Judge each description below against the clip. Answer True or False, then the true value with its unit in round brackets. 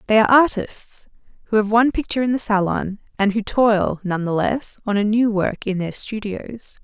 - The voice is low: False (215 Hz)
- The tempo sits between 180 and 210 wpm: True (200 wpm)